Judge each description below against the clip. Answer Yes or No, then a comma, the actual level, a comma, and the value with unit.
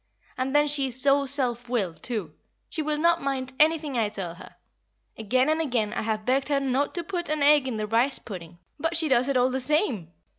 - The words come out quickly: Yes, fast, 225 wpm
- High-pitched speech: Yes, very high, 265 Hz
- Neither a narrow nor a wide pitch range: Yes, average, 4.4 semitones